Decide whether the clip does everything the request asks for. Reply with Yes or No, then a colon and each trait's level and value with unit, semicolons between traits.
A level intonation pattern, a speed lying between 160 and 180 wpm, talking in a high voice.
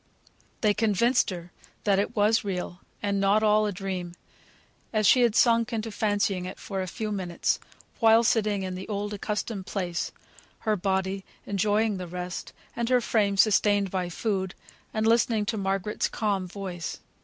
Yes: narrow, 2.3 semitones; average, 165 wpm; high, 205 Hz